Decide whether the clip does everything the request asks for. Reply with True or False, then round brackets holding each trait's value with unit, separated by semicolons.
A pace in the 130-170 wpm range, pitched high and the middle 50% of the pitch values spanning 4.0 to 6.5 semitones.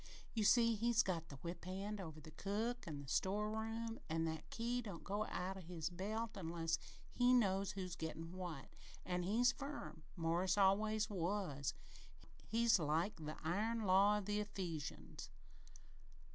True (155 wpm; 195 Hz; 4.6 semitones)